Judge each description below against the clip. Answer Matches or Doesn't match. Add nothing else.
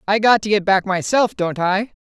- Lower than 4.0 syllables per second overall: Doesn't match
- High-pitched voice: Matches